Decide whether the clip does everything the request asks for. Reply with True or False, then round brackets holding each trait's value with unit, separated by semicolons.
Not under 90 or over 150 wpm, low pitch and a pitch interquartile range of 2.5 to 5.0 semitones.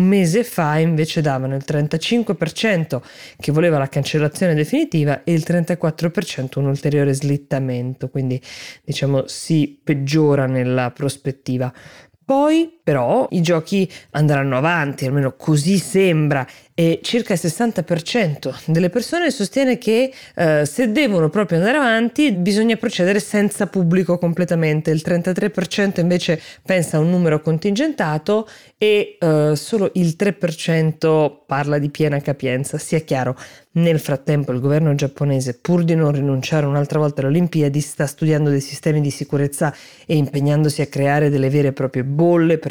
False (140 wpm; 155 Hz; 4.1 semitones)